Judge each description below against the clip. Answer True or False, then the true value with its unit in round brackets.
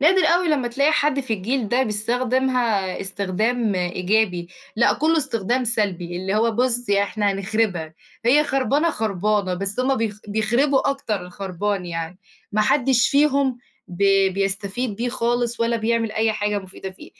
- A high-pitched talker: True (220 Hz)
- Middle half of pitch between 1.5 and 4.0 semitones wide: False (4.5 semitones)